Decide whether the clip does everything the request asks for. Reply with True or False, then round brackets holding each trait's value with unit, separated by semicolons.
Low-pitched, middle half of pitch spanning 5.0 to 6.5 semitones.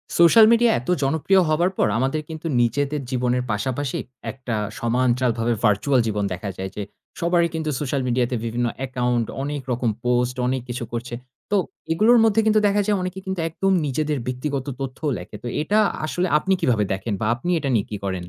True (130 Hz; 5.3 semitones)